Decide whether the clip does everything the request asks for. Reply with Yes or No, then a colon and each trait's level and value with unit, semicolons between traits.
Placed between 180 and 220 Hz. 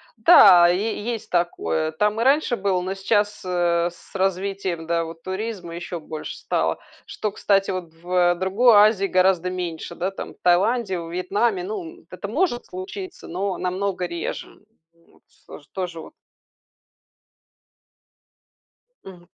Yes: medium, 185 Hz